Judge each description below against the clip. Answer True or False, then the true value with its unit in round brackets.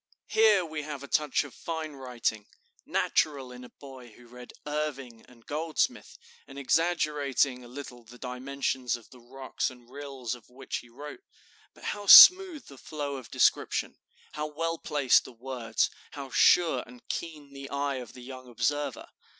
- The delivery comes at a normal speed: True (170 wpm)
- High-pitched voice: False (135 Hz)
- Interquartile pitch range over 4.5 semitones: False (3.2 semitones)